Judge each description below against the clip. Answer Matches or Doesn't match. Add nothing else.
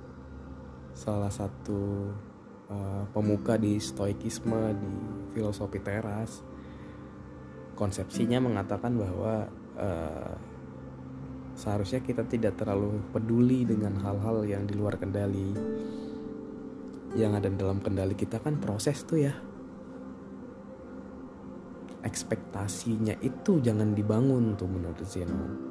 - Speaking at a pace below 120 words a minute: Matches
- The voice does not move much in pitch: Doesn't match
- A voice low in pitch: Matches